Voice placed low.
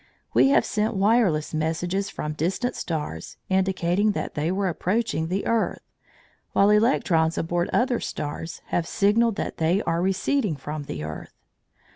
No: medium, 185 Hz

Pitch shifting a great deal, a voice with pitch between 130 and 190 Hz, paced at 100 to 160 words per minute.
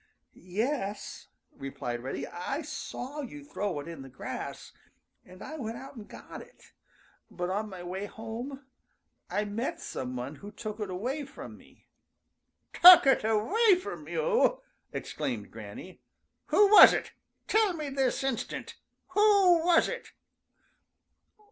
No: wide, 8.8 semitones; high, 240 Hz; average, 140 wpm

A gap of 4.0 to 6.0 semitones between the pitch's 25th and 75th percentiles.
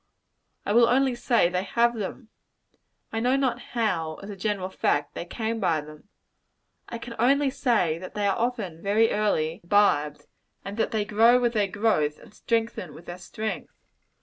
Yes: average, 4.4 semitones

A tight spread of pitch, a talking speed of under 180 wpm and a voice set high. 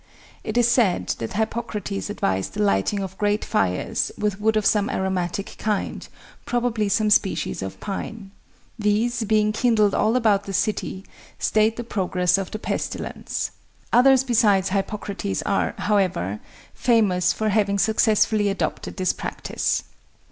Yes: narrow, 2.2 semitones; average, 140 wpm; high, 210 Hz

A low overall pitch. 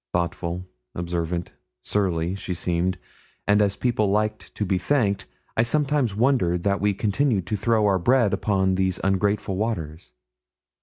Yes: low, 100 Hz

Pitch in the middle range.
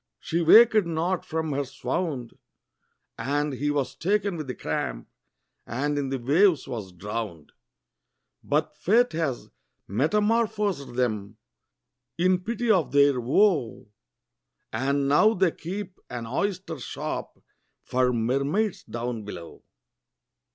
Yes: medium, 145 Hz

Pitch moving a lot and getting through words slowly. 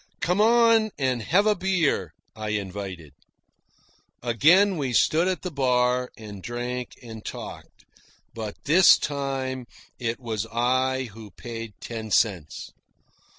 Yes: wide, 5.7 semitones; slow, 125 wpm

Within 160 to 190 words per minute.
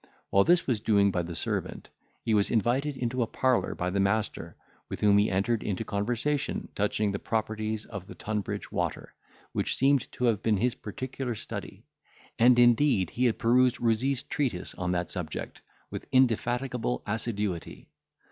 Yes: average, 165 wpm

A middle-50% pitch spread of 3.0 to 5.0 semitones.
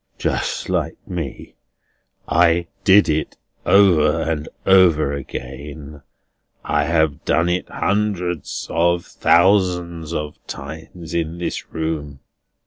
No: narrow, 2.5 semitones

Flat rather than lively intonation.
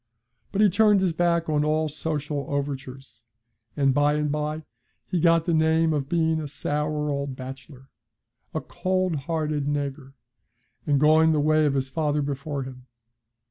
Yes: narrow, 2.3 semitones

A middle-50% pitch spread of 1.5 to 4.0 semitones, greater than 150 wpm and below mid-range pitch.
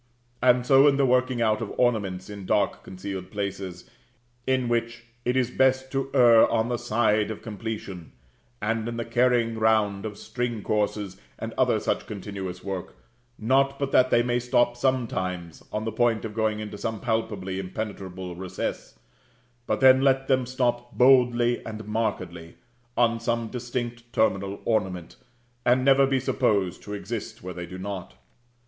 Yes: average, 3.6 semitones; average, 160 wpm; low, 115 Hz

